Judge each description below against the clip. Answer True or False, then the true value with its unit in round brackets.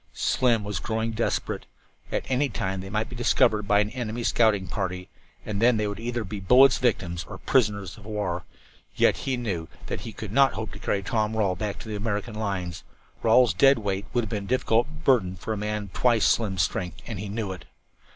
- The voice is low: True (105 Hz)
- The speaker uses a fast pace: True (215 wpm)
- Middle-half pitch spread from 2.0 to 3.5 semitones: True (3.0 semitones)